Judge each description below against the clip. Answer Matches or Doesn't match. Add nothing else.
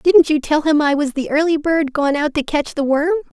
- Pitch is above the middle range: Matches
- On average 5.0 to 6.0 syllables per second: Matches